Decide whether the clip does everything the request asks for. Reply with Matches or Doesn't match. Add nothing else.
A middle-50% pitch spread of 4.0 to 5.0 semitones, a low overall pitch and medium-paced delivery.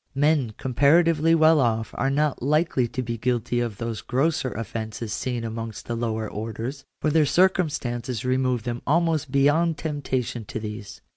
Matches